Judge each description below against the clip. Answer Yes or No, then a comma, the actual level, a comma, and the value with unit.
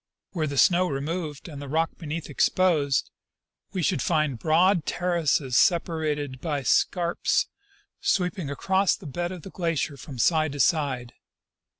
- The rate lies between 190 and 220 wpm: No, average, 150 wpm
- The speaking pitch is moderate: Yes, medium, 160 Hz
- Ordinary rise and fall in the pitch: Yes, average, 3.6 semitones